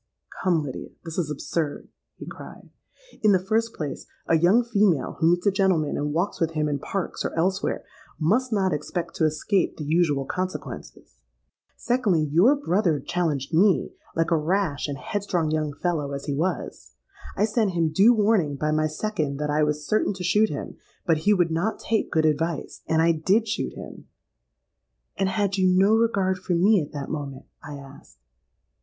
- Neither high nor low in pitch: Yes, medium, 170 Hz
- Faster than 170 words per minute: Yes, average, 180 wpm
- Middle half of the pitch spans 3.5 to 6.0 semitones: Yes, average, 4.6 semitones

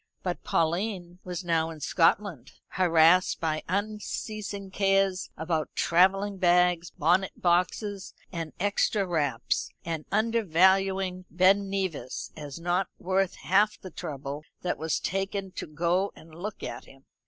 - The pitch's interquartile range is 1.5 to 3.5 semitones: Yes, average, 2.9 semitones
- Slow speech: Yes, slow, 130 wpm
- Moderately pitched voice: Yes, medium, 180 Hz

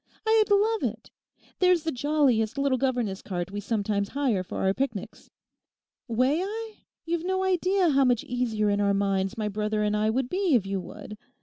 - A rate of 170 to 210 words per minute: Yes, average, 185 wpm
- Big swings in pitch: Yes, wide, 8.1 semitones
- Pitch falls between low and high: No, high, 245 Hz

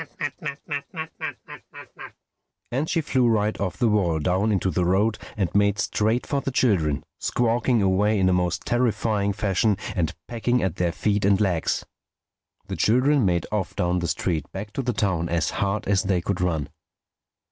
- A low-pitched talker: Yes, low, 100 Hz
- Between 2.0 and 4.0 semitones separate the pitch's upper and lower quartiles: Yes, average, 3.7 semitones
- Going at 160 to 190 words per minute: Yes, average, 165 wpm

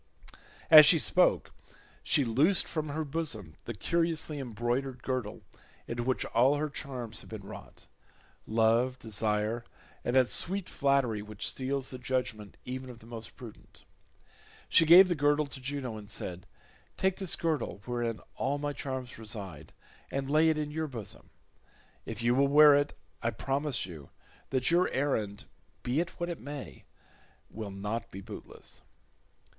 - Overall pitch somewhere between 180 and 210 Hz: No, low, 130 Hz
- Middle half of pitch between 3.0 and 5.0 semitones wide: Yes, average, 4.6 semitones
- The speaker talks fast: No, average, 155 wpm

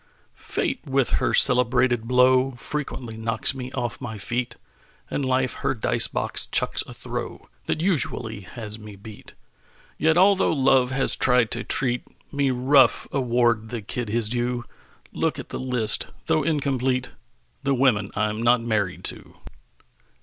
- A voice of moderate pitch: No, low, 125 Hz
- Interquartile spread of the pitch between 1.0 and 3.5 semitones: Yes, average, 2.8 semitones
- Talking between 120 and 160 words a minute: Yes, average, 150 wpm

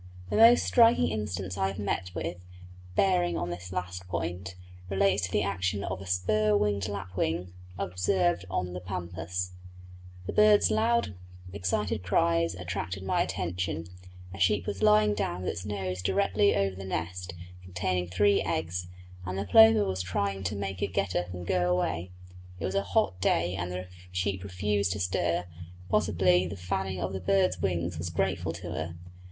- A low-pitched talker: Yes, very low, 90 Hz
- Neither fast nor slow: Yes, average, 170 wpm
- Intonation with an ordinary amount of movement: No, narrow, 1.8 semitones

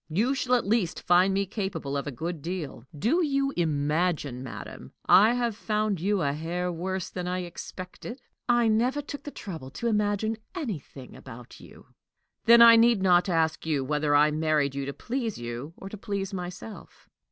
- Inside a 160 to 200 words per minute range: Yes, average, 180 wpm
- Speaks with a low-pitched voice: No, medium, 185 Hz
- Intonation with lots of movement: Yes, wide, 6.3 semitones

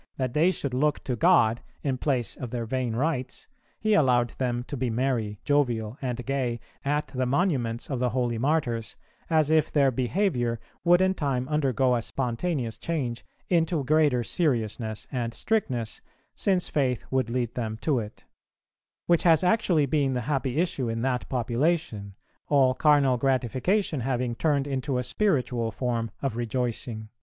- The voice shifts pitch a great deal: No, average, 4.0 semitones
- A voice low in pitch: Yes, low, 130 Hz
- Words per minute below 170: Yes, average, 160 wpm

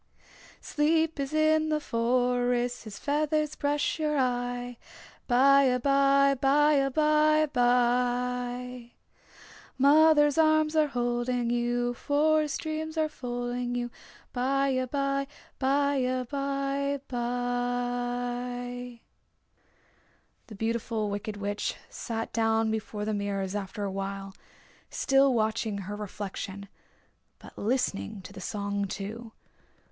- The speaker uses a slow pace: Yes, slow, 105 wpm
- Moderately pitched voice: No, high, 245 Hz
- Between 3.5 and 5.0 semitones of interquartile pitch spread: No, average, 3.1 semitones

